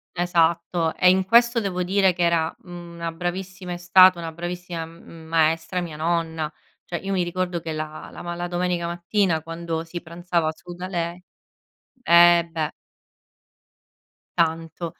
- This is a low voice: No, medium, 175 Hz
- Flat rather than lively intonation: Yes, narrow, 1.4 semitones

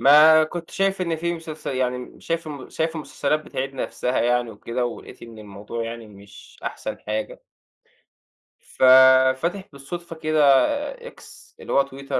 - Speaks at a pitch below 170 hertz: Yes, medium, 140 Hz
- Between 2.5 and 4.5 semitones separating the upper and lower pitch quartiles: No, average, 5.2 semitones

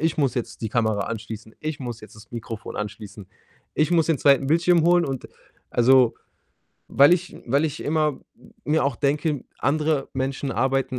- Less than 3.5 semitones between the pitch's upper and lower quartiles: No, average, 4.7 semitones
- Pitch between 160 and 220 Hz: No, low, 135 Hz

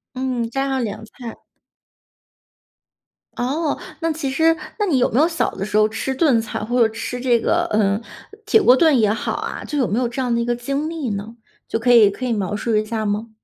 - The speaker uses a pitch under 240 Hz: No, high, 245 Hz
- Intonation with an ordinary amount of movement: Yes, average, 3.8 semitones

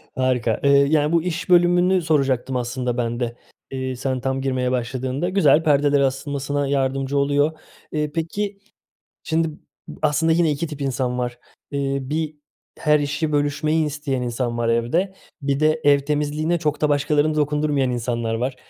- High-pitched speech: No, medium, 145 Hz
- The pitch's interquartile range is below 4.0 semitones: Yes, average, 3.0 semitones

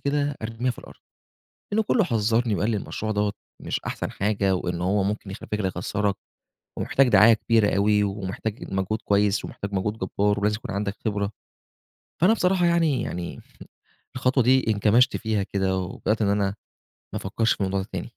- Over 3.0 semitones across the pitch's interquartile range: No, average, 2.7 semitones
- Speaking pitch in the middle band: No, low, 105 Hz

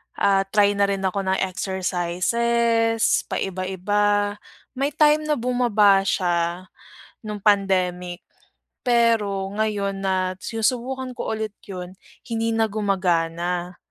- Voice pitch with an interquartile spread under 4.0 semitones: Yes, average, 3.4 semitones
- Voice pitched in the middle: No, high, 200 Hz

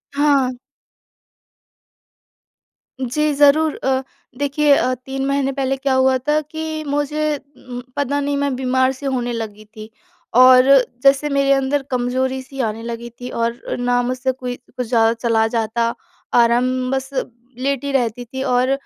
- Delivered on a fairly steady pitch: Yes, narrow, 2.2 semitones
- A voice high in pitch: Yes, very high, 260 Hz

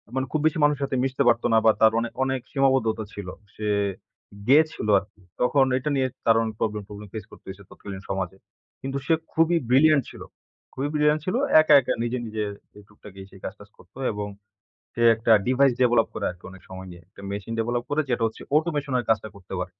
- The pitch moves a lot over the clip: No, average, 4.8 semitones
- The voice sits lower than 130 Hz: Yes, low, 120 Hz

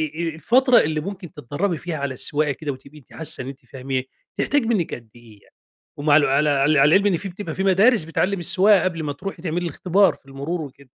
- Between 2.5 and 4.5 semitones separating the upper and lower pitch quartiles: No, average, 5.2 semitones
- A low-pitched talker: No, medium, 160 Hz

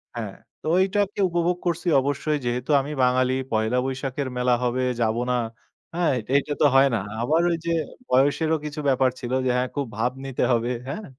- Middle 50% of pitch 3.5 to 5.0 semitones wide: Yes, average, 4.1 semitones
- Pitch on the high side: No, low, 135 Hz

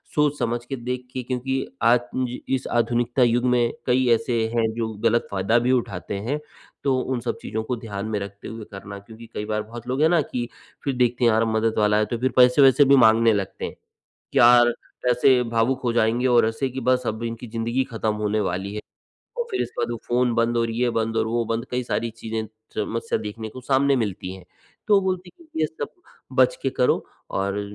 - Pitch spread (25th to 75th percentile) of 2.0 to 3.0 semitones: Yes, narrow, 2.4 semitones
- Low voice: Yes, low, 120 Hz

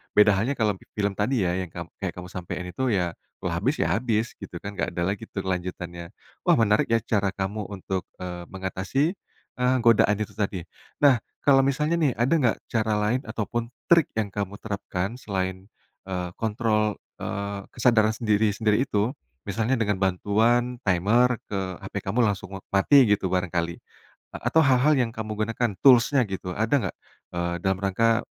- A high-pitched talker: No, low, 105 Hz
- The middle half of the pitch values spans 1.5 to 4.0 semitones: Yes, average, 3.6 semitones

